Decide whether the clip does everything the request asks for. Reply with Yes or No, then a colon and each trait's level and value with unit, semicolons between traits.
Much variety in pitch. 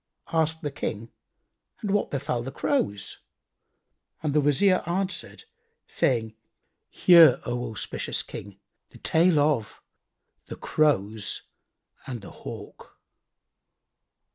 Yes: wide, 6.3 semitones